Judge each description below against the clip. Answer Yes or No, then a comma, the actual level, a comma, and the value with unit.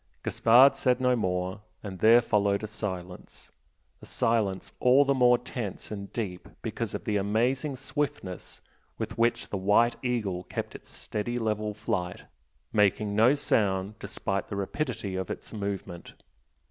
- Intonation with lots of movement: No, average, 3.7 semitones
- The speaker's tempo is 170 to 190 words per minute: No, average, 145 wpm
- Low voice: Yes, low, 105 Hz